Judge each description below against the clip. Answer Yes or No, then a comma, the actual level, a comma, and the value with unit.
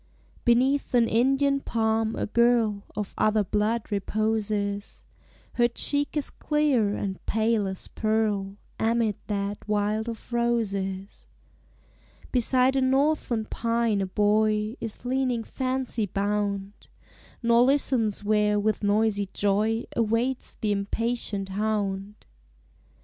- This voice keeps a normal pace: No, slow, 110 wpm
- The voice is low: No, high, 220 Hz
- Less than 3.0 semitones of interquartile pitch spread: Yes, narrow, 2.5 semitones